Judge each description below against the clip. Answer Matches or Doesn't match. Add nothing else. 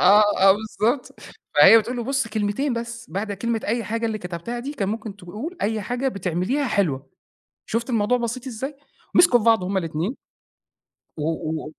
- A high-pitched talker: Matches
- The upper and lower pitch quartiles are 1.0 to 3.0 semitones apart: Doesn't match